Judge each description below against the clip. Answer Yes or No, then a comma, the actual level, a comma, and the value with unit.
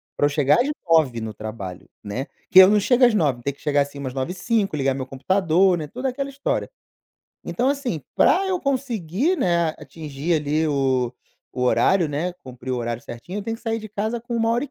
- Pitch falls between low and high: Yes, medium, 165 Hz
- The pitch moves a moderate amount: No, wide, 8.8 semitones